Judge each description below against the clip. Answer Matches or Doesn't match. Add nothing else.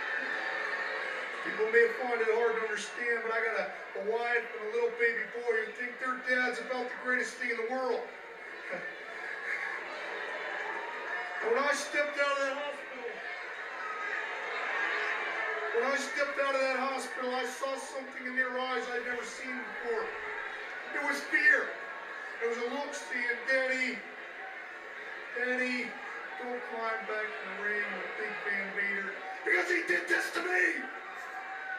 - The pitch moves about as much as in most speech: Matches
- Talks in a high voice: Matches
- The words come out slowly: Doesn't match